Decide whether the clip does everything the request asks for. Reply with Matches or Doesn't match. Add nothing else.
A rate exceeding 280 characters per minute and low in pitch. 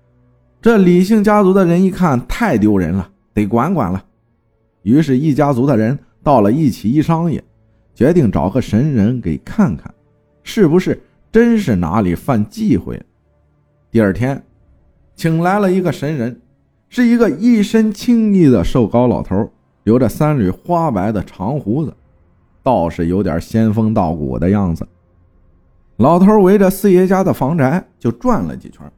Doesn't match